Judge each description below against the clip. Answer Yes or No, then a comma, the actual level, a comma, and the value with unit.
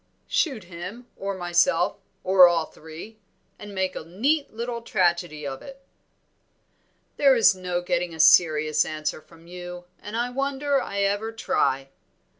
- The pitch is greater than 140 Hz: Yes, medium, 185 Hz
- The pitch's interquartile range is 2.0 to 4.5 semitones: No, average, 5.0 semitones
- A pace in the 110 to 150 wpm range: Yes, average, 145 wpm